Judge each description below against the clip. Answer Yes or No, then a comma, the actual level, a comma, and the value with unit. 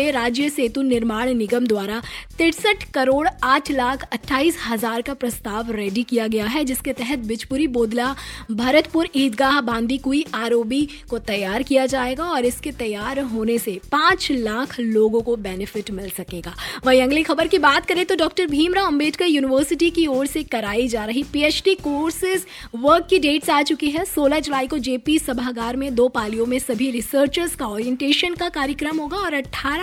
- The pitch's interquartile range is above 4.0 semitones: Yes, average, 4.4 semitones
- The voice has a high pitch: Yes, very high, 270 Hz